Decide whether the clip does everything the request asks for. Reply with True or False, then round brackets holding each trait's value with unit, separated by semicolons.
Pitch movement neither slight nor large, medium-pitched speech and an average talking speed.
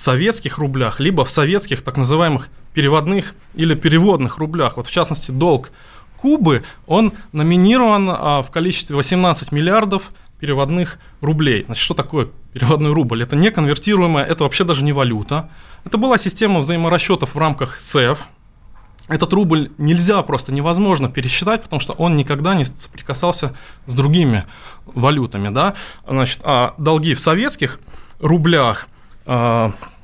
True (4.6 semitones; 155 Hz; 135 wpm)